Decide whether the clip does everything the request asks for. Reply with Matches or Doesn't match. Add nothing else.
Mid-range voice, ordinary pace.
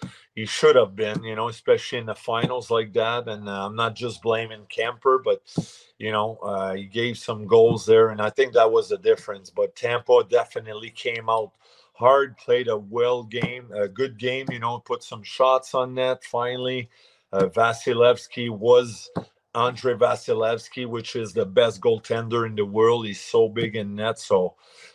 Doesn't match